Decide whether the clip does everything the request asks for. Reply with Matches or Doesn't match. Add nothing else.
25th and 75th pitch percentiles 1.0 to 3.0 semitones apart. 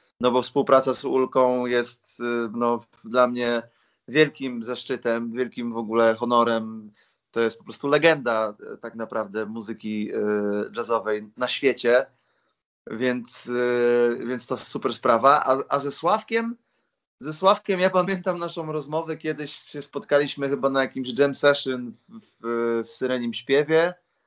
Doesn't match